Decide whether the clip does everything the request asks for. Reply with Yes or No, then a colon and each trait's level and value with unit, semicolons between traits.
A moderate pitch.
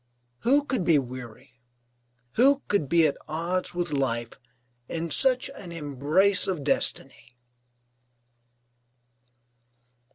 Yes: medium, 165 Hz